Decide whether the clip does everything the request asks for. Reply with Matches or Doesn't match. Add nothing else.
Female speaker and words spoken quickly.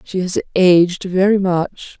Doesn't match